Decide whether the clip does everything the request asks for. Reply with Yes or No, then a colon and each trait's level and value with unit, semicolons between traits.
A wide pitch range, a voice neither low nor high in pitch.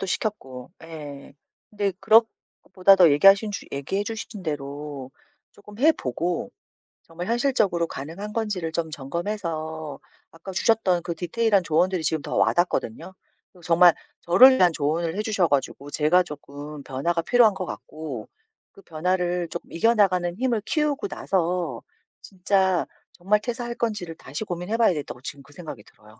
No: average, 4.8 semitones; medium, 175 Hz